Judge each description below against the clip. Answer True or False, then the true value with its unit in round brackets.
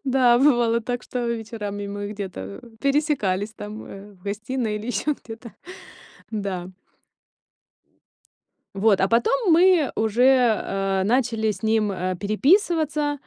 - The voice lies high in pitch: True (220 Hz)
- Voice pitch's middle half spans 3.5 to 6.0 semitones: True (4.4 semitones)